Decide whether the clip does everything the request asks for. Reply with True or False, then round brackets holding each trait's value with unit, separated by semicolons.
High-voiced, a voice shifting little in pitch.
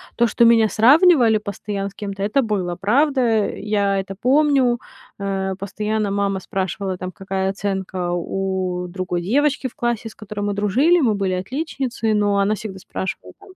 False (205 Hz; 3.6 semitones)